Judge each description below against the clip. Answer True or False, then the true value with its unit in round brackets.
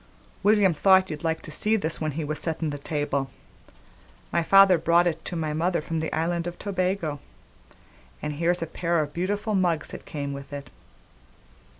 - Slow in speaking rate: False (185 wpm)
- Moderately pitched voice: True (165 Hz)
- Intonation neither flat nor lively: True (3.2 semitones)